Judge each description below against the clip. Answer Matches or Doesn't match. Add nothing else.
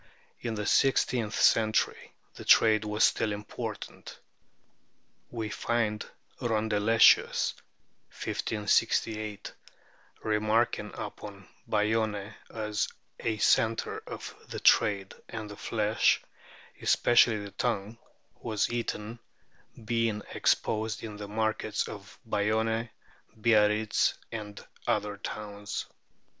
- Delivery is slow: Matches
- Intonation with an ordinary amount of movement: Doesn't match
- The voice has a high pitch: Doesn't match